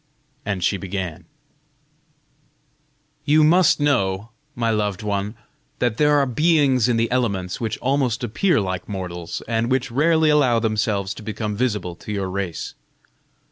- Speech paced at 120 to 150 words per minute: Yes, average, 140 wpm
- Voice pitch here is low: Yes, low, 115 Hz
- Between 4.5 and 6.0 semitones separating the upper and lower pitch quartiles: Yes, average, 5.0 semitones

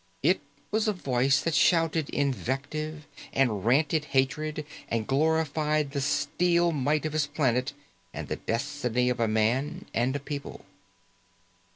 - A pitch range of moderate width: Yes, average, 3.2 semitones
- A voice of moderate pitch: Yes, medium, 145 Hz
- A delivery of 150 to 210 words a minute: No, average, 140 wpm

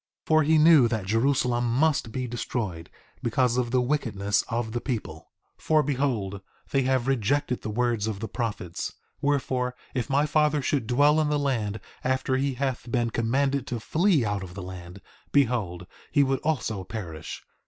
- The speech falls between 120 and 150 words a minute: No, average, 175 wpm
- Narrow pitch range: No, average, 4.3 semitones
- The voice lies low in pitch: Yes, low, 125 Hz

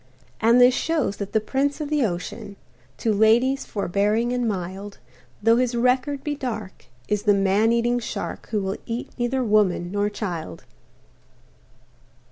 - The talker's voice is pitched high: Yes, high, 220 Hz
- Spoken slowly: No, average, 150 wpm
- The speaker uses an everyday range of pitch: Yes, average, 3.7 semitones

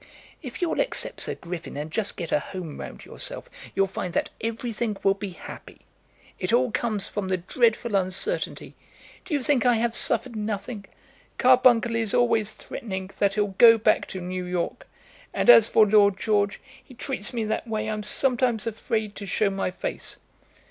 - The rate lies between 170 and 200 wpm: Yes, average, 175 wpm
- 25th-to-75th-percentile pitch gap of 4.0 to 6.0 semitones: No, average, 3.4 semitones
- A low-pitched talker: No, high, 215 Hz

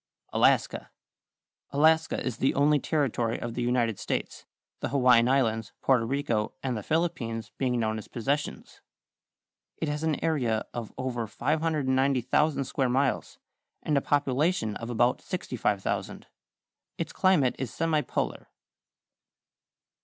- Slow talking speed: Yes, slow, 125 wpm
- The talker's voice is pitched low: Yes, low, 130 Hz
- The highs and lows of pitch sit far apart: No, average, 4.0 semitones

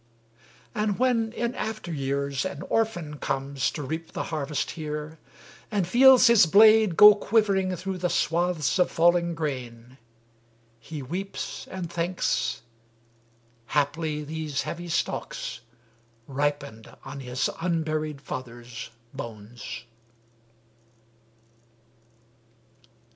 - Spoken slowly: Yes, slow, 100 wpm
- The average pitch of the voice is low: No, medium, 160 Hz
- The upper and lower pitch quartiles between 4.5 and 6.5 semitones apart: Yes, average, 5.0 semitones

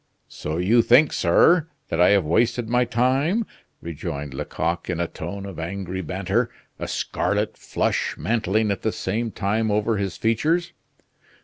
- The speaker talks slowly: No, average, 150 wpm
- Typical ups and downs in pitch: Yes, average, 4.9 semitones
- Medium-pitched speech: No, low, 105 Hz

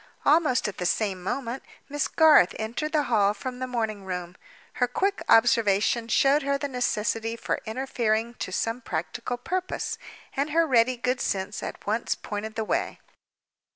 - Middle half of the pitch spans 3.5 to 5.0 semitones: Yes, average, 4.1 semitones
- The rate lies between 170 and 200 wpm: No, average, 160 wpm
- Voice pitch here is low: No, high, 235 Hz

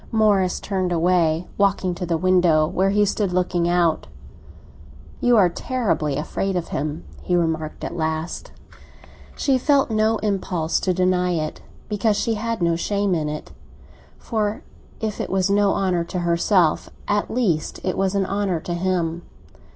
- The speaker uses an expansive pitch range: No, average, 3.2 semitones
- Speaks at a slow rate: No, average, 160 wpm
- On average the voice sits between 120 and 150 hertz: No, medium, 185 Hz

